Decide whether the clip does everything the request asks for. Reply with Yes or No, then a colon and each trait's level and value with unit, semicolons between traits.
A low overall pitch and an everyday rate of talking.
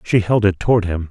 No: low, 100 Hz; fast, 270 wpm